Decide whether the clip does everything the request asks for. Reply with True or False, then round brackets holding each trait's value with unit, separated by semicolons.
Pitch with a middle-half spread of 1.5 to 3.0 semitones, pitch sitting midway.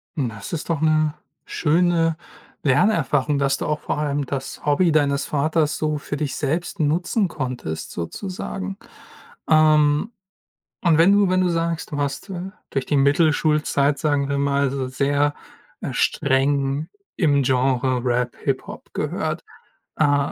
True (2.6 semitones; 145 Hz)